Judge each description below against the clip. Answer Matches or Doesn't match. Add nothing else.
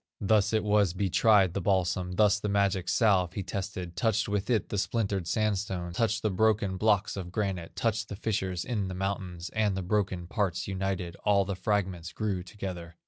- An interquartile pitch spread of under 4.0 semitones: Matches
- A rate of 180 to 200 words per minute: Matches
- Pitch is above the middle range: Doesn't match